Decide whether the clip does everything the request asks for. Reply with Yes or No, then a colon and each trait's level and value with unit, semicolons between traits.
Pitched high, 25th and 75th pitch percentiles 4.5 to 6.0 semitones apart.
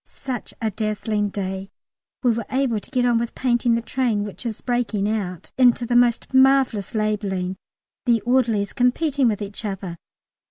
No: high, 225 Hz; average, 3.1 semitones